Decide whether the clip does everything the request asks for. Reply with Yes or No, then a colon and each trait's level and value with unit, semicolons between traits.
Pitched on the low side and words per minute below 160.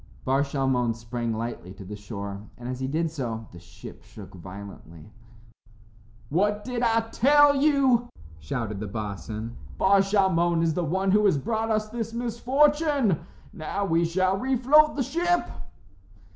No: medium, 170 Hz; average, 150 wpm